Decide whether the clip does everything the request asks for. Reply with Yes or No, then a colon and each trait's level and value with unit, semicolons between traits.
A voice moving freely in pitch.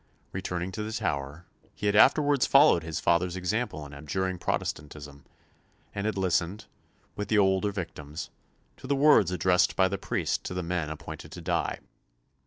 No: average, 4.0 semitones